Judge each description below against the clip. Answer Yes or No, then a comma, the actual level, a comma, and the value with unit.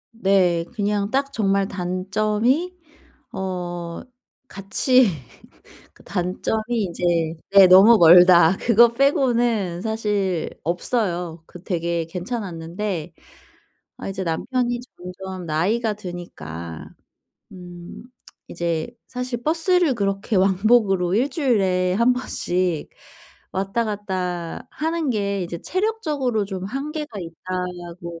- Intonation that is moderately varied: Yes, average, 4.9 semitones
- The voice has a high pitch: Yes, high, 195 Hz